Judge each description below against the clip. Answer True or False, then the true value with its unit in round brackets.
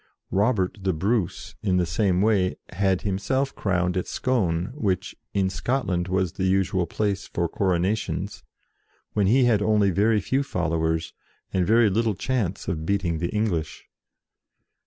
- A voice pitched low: True (95 Hz)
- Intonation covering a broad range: False (3.3 semitones)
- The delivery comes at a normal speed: True (145 wpm)